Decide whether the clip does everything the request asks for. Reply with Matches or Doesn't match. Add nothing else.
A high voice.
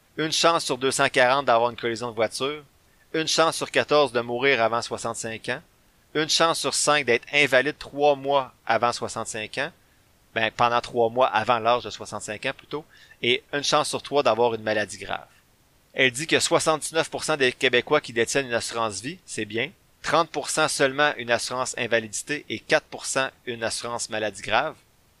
Doesn't match